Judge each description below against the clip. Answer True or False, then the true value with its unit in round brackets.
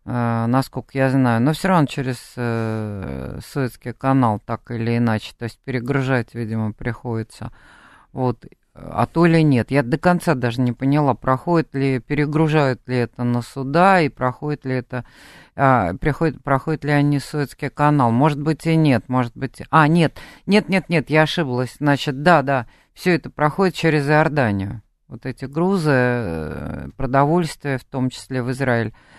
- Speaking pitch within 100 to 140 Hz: True (135 Hz)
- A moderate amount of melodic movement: True (4.0 semitones)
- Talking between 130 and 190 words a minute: True (160 wpm)